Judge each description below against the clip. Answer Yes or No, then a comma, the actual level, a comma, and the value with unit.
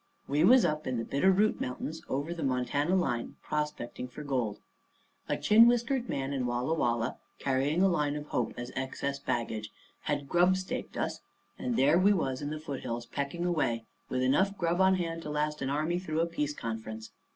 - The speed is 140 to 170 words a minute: No, average, 190 wpm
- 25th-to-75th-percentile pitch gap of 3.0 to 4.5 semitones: No, average, 5.1 semitones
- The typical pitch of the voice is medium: Yes, medium, 150 Hz